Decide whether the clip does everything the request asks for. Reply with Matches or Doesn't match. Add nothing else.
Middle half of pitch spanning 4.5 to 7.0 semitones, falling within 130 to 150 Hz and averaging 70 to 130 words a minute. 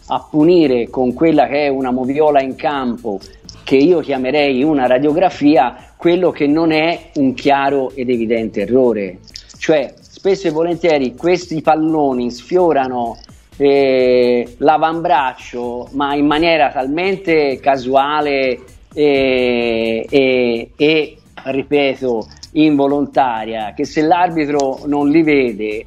Doesn't match